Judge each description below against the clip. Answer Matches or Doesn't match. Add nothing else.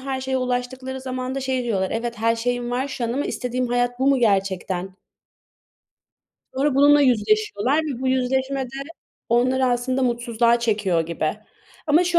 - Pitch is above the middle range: Matches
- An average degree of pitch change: Doesn't match